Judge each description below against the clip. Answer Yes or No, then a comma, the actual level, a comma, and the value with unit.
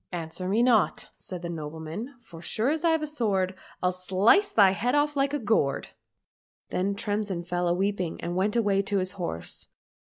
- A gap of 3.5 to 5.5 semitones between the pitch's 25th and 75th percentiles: Yes, average, 4.8 semitones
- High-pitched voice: Yes, high, 195 Hz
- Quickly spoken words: Yes, fast, 215 wpm